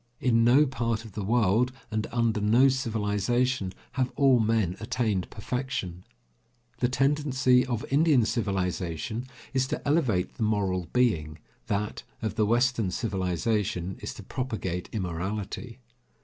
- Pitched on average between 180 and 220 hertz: No, low, 110 Hz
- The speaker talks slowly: Yes, slow, 130 wpm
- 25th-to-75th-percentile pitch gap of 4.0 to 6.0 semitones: Yes, average, 4.5 semitones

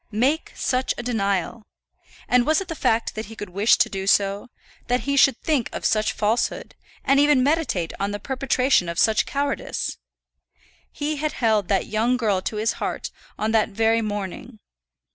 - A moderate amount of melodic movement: Yes, average, 4.7 semitones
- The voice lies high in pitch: Yes, high, 225 Hz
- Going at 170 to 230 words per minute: Yes, average, 180 wpm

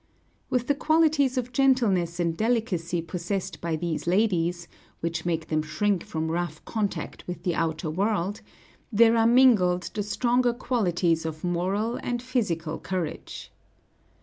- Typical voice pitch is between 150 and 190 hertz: Yes, medium, 185 Hz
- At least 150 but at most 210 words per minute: No, average, 140 wpm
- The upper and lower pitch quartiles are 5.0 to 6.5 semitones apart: Yes, wide, 5.6 semitones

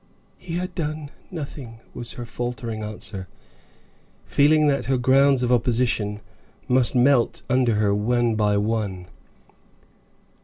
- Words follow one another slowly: Yes, slow, 120 wpm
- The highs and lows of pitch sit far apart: No, average, 4.1 semitones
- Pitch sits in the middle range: No, low, 120 Hz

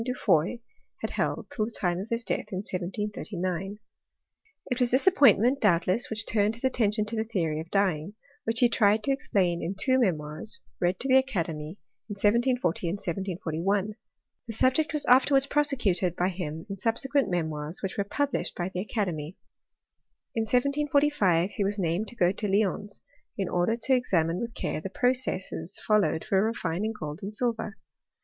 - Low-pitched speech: No, high, 205 Hz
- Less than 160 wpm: No, average, 170 wpm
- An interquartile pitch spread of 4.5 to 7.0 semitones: Yes, average, 5.1 semitones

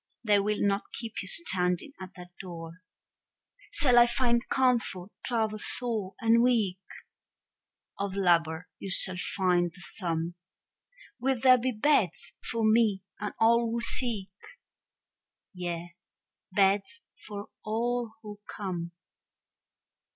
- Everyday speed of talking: No, slow, 120 wpm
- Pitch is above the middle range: Yes, high, 205 Hz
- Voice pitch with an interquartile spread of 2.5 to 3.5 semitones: No, average, 4.4 semitones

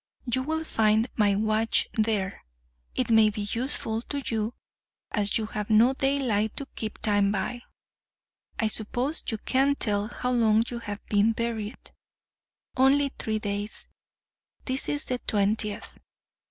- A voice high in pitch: Yes, high, 220 Hz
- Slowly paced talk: Yes, slow, 130 wpm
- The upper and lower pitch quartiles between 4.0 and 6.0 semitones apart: No, average, 3.1 semitones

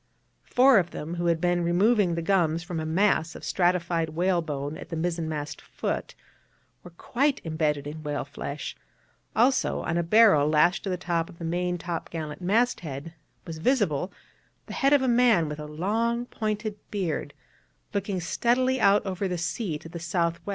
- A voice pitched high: No, medium, 175 Hz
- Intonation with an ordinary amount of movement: Yes, average, 4.1 semitones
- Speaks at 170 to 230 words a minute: Yes, average, 180 wpm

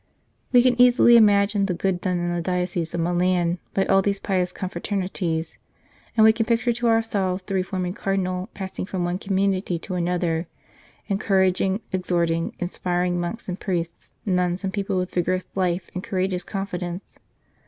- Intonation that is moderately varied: No, narrow, 1.9 semitones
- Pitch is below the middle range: No, medium, 185 Hz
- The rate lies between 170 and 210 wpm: No, average, 160 wpm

